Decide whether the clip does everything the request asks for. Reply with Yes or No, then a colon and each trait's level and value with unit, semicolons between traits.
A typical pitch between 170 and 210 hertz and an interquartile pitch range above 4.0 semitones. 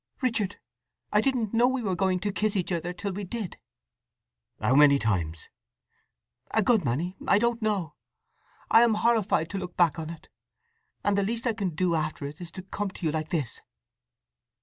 Yes: high, 190 Hz; average, 5.1 semitones